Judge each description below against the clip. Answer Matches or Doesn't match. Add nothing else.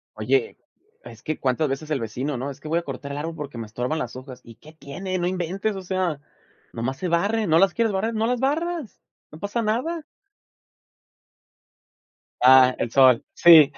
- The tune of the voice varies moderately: Doesn't match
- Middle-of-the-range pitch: Matches